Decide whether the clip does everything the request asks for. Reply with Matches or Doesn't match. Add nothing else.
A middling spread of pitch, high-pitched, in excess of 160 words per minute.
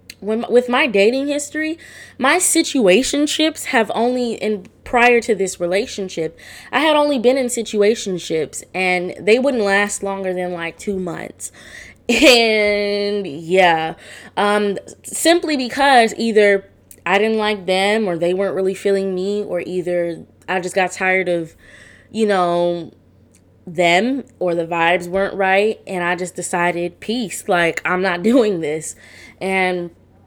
Doesn't match